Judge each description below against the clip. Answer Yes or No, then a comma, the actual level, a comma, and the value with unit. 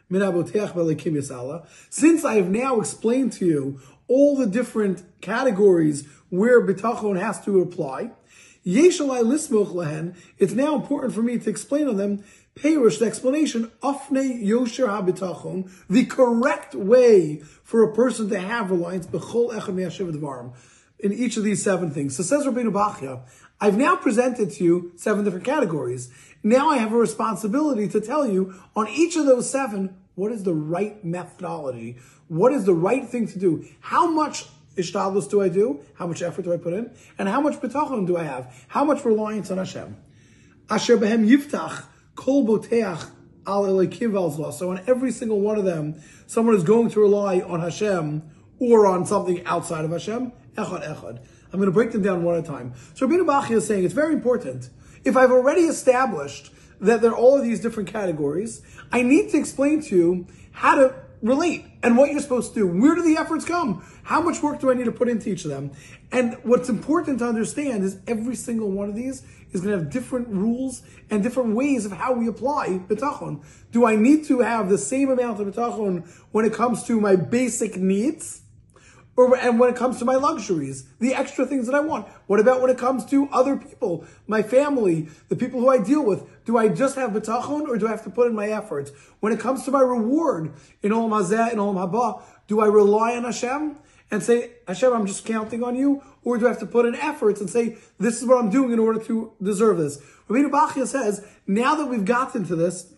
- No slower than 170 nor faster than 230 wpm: Yes, average, 190 wpm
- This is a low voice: No, high, 220 Hz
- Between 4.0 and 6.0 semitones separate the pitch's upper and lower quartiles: Yes, wide, 5.4 semitones